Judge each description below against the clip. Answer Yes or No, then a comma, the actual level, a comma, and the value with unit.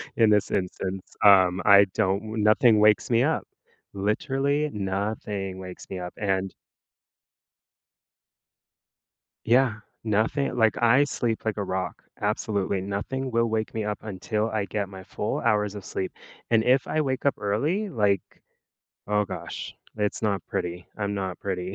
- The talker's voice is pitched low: Yes, low, 105 Hz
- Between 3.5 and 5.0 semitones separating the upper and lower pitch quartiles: No, average, 2.9 semitones